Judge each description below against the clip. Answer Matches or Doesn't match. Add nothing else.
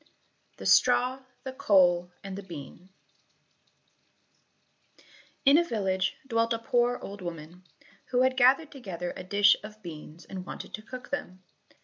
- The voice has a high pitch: Matches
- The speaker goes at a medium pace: Matches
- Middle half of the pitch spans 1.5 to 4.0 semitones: Doesn't match